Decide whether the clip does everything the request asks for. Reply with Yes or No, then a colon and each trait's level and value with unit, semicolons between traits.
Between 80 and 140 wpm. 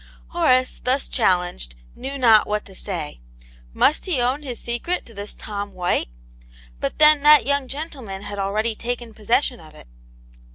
No: average, 170 wpm